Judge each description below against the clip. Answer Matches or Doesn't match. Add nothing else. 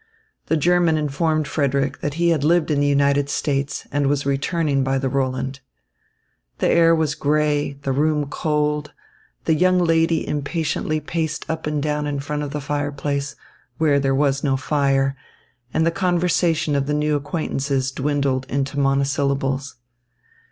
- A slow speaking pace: Doesn't match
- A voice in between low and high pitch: Matches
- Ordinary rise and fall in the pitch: Doesn't match